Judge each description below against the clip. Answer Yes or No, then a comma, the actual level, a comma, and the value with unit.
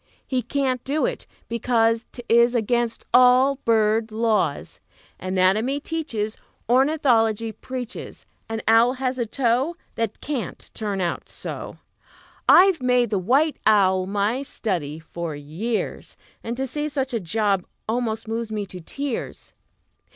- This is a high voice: Yes, high, 230 Hz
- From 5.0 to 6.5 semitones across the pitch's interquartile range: No, average, 3.3 semitones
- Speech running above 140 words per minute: No, slow, 135 wpm